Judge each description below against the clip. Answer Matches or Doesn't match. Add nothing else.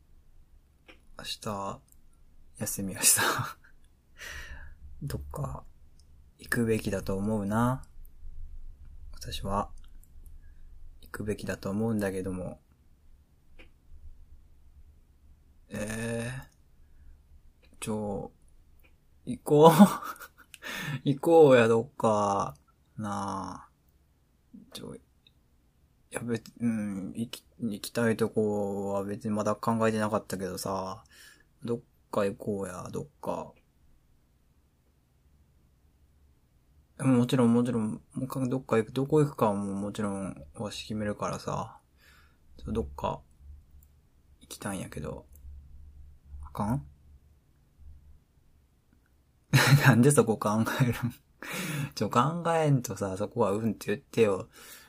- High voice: Doesn't match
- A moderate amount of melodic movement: Doesn't match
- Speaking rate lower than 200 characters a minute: Matches